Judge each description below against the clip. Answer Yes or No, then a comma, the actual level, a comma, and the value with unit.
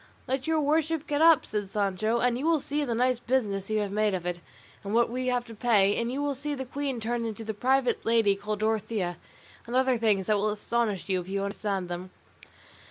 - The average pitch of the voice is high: Yes, high, 230 Hz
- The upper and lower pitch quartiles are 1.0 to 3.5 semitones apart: No, average, 4.2 semitones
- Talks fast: Yes, fast, 230 wpm